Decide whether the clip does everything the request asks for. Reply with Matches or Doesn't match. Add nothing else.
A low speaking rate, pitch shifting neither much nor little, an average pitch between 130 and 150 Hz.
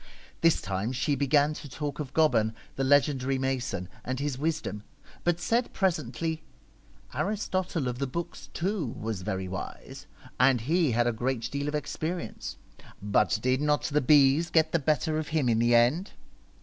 Doesn't match